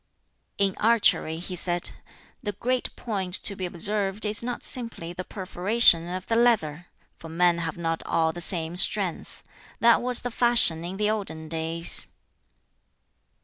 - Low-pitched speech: No, medium, 185 Hz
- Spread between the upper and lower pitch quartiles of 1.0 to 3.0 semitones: No, average, 4.4 semitones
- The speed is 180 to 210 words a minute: No, average, 150 wpm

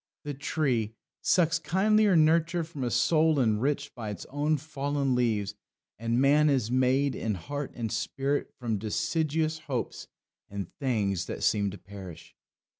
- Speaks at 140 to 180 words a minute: Yes, average, 145 wpm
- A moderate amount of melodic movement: No, wide, 5.8 semitones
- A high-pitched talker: No, low, 135 Hz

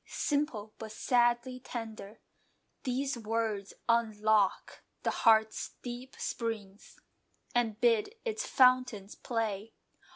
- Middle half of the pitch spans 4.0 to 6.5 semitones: No, average, 2.7 semitones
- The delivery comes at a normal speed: No, slow, 95 wpm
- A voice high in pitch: Yes, high, 230 Hz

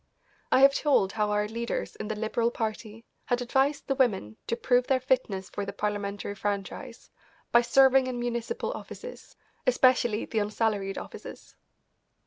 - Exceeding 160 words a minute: No, average, 150 wpm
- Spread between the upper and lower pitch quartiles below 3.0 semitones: No, average, 3.4 semitones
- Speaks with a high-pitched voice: Yes, high, 230 Hz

